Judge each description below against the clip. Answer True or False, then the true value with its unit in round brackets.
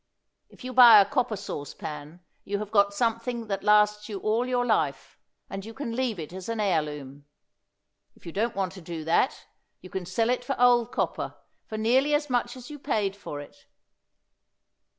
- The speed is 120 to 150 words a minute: False (190 wpm)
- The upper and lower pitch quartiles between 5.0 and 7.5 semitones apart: False (4.4 semitones)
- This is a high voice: True (215 Hz)